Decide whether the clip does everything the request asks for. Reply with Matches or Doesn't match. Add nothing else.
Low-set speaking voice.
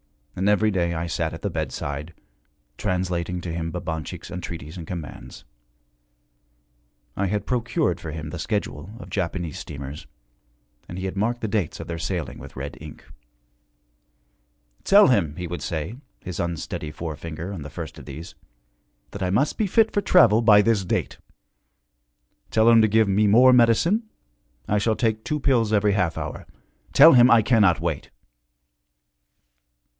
Matches